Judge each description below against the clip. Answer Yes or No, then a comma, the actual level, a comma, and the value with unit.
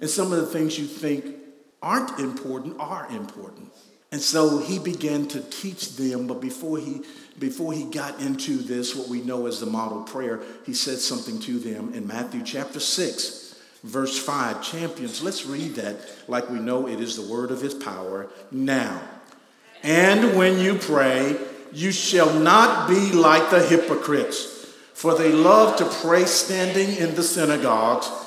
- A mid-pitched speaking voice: Yes, medium, 155 Hz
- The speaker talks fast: No, average, 170 wpm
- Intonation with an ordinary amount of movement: No, wide, 6.1 semitones